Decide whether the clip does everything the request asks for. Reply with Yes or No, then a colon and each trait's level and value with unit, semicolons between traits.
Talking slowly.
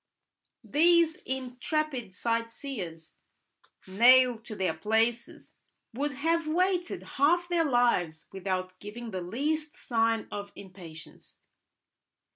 Yes: slow, 95 wpm